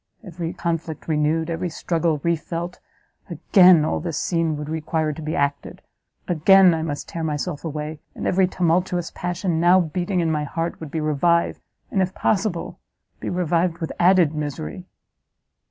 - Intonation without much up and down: Yes, narrow, 2.3 semitones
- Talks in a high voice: No, medium, 165 Hz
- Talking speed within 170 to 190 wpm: No, average, 160 wpm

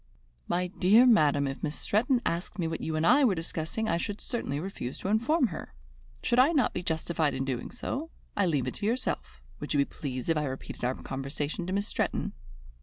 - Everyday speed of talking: No, fast, 215 wpm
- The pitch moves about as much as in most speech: No, wide, 7.2 semitones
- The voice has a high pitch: No, medium, 170 Hz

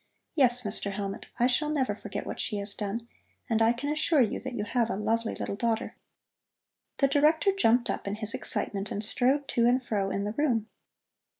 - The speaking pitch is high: Yes, high, 235 Hz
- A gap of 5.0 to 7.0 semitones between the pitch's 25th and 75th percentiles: No, average, 3.9 semitones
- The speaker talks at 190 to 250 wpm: Yes, average, 200 wpm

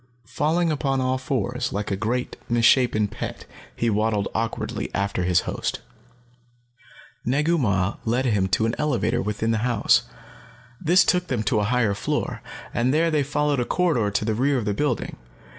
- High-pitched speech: No, low, 120 Hz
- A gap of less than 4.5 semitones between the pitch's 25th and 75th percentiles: No, average, 5.0 semitones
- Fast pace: No, average, 170 wpm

